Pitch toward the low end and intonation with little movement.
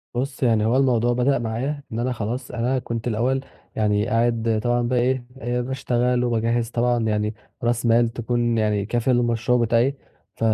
Yes: low, 120 Hz; narrow, 1.5 semitones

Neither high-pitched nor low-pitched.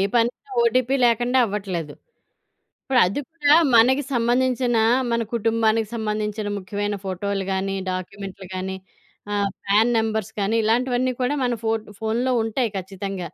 No: high, 220 Hz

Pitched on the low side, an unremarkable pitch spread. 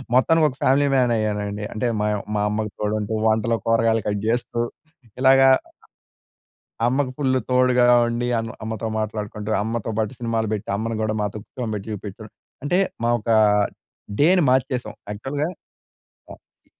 Yes: low, 115 Hz; average, 3.1 semitones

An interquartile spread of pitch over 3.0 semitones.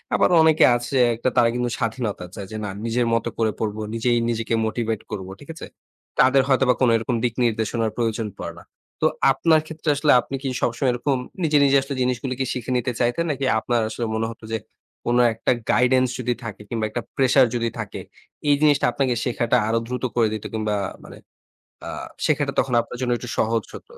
No: narrow, 2.6 semitones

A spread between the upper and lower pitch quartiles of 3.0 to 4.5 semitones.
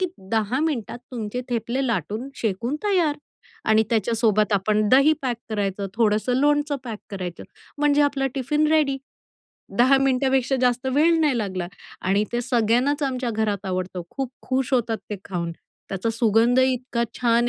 Yes: average, 4.1 semitones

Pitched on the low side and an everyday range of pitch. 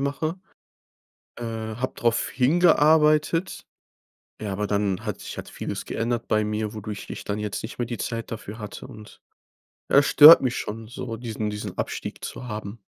Yes: low, 115 Hz; average, 3.6 semitones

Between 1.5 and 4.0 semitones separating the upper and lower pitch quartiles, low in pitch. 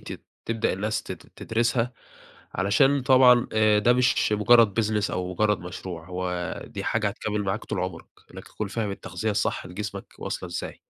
Yes: average, 3.6 semitones; low, 105 Hz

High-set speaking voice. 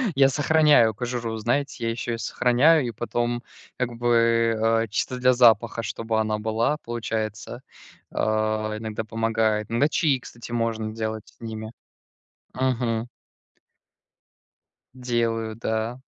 No: low, 115 Hz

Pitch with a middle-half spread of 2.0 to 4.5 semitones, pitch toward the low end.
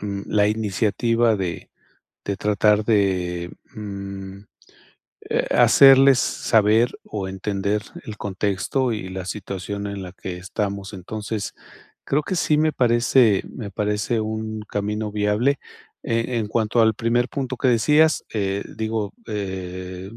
Yes: average, 2.8 semitones; low, 105 Hz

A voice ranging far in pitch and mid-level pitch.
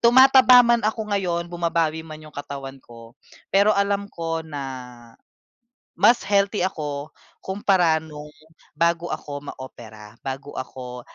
Yes: wide, 5.8 semitones; medium, 165 Hz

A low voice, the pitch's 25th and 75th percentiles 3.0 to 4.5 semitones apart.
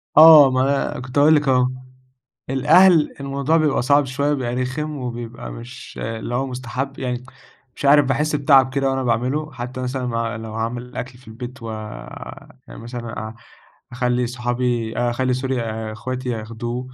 No: low, 125 Hz; narrow, 2.4 semitones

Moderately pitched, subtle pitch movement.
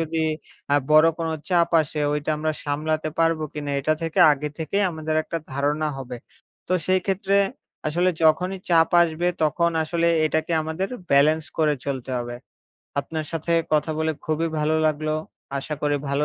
Yes: medium, 155 Hz; narrow, 1.7 semitones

